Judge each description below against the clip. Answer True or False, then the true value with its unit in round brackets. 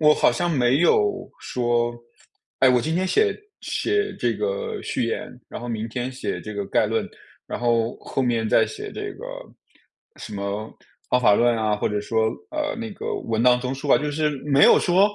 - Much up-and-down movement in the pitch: True (8.0 semitones)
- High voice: False (125 Hz)